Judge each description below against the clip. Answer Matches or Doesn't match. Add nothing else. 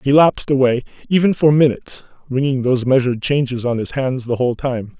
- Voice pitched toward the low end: Matches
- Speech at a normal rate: Matches